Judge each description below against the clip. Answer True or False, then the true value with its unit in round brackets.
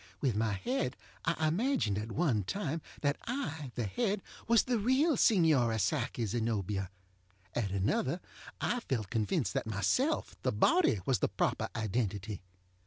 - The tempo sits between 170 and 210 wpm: False (140 wpm)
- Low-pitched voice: True (130 Hz)